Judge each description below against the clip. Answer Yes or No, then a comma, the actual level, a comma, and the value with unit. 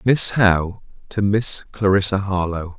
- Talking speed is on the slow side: Yes, slow, 130 wpm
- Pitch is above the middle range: No, low, 100 Hz